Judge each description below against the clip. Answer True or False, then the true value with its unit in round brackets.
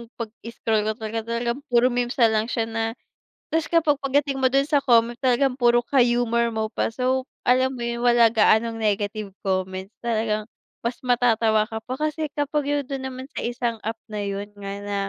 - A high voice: True (235 Hz)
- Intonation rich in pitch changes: False (2.8 semitones)